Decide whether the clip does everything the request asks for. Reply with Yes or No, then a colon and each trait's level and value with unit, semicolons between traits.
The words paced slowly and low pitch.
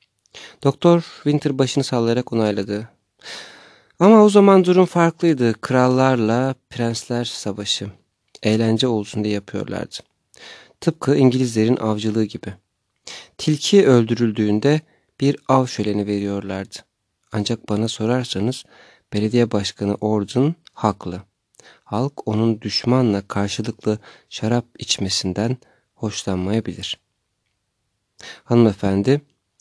Yes: slow, 85 wpm; low, 115 Hz